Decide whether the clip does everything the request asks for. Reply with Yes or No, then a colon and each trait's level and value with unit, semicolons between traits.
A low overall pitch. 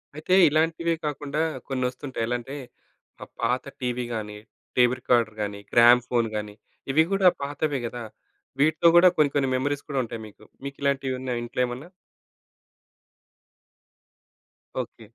Yes: low, 130 Hz